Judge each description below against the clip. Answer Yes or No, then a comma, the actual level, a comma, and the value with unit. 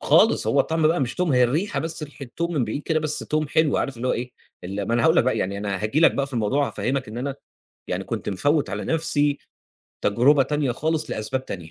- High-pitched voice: No, medium, 140 Hz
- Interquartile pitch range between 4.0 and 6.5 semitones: Yes, average, 4.5 semitones